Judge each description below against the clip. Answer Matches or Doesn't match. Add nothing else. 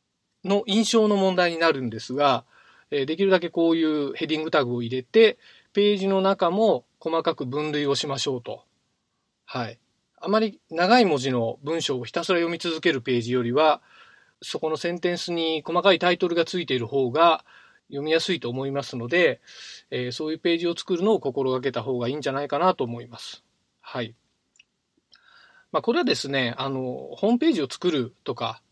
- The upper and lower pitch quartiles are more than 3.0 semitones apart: Matches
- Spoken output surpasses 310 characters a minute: Matches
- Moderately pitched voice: Matches